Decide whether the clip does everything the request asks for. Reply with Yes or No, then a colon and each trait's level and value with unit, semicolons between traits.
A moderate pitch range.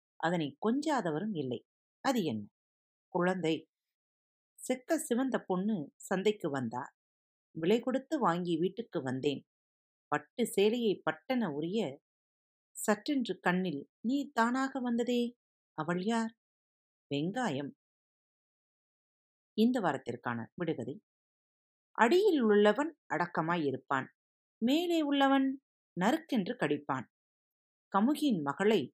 No: wide, 8.7 semitones